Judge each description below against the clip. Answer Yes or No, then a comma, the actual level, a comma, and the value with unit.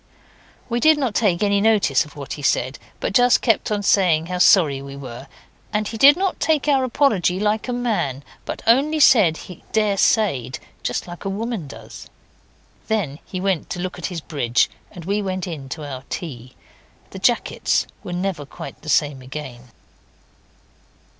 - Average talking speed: Yes, average, 175 wpm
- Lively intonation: Yes, wide, 7.1 semitones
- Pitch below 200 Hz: Yes, medium, 185 Hz